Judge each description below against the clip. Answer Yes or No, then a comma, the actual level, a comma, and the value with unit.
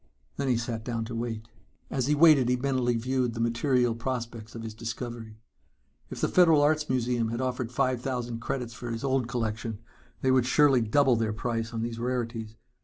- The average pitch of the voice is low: Yes, low, 120 Hz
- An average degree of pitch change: No, narrow, 2.1 semitones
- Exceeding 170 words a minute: Yes, average, 190 wpm